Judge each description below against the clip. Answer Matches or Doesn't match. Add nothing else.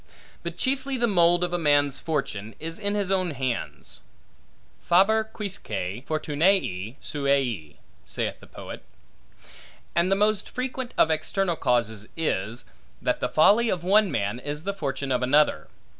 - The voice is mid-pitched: Matches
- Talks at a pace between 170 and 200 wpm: Doesn't match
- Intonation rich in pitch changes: Matches